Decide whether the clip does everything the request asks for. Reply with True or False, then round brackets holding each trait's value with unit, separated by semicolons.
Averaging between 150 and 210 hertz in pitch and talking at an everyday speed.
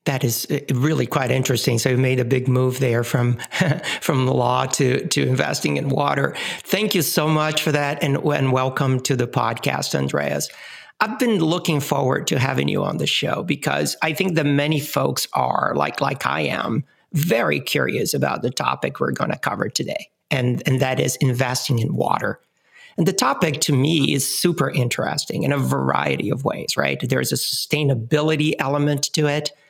False (140 Hz; 190 wpm)